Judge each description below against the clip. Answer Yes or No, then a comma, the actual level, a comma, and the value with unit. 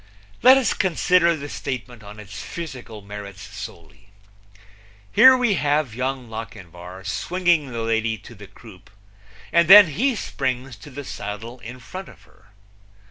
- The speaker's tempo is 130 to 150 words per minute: Yes, average, 145 wpm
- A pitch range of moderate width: No, wide, 7.9 semitones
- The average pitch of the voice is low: Yes, low, 125 Hz